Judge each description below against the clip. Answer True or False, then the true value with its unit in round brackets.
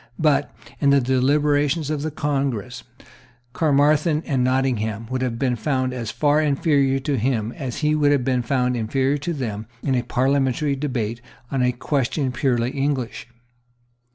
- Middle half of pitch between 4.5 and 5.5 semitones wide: False (2.7 semitones)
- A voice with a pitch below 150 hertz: True (135 Hz)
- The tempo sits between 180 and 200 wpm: False (155 wpm)